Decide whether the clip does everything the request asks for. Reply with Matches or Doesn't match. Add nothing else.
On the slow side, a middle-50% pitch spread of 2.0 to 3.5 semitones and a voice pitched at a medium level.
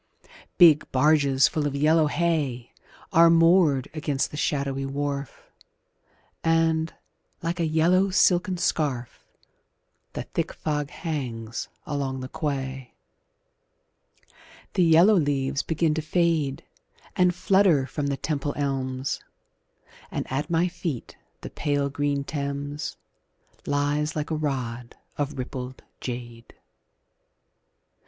Matches